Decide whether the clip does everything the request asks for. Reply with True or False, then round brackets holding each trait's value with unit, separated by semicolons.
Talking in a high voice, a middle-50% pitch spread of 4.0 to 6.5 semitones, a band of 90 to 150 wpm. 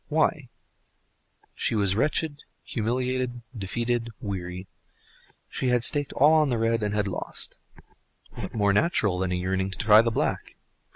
False (115 Hz; 4.4 semitones; 140 wpm)